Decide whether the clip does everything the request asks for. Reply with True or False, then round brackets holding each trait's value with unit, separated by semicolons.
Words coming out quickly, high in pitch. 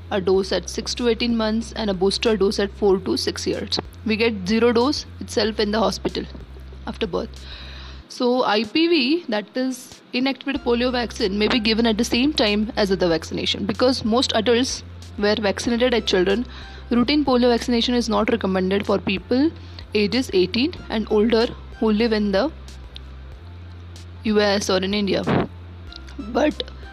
False (160 wpm; 215 Hz)